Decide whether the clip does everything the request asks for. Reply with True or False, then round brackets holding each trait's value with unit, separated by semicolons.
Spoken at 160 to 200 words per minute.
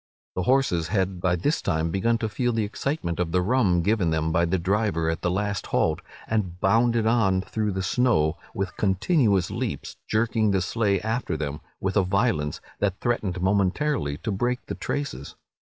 True (180 wpm)